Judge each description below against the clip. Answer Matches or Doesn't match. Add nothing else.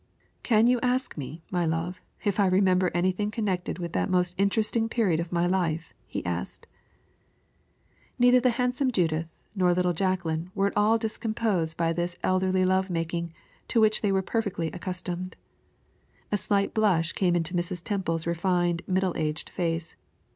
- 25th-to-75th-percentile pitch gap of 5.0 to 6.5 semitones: Doesn't match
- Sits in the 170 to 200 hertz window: Matches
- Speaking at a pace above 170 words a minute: Doesn't match